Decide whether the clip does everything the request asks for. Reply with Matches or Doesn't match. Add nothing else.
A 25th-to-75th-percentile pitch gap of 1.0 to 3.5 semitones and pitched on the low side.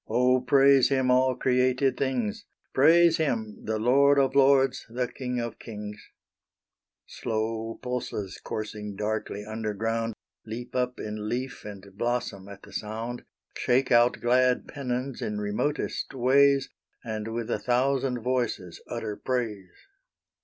Matches